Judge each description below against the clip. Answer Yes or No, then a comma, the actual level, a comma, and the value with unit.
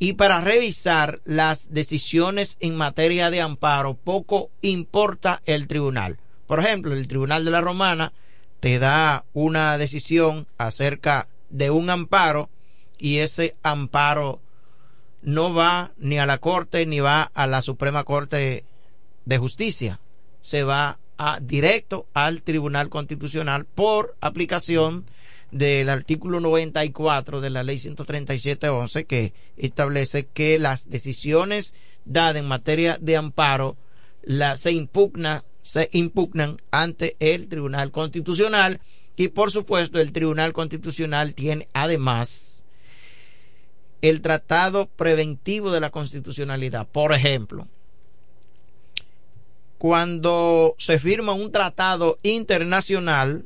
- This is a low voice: No, medium, 155 Hz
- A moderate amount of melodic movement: Yes, average, 3.2 semitones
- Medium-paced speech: No, slow, 115 wpm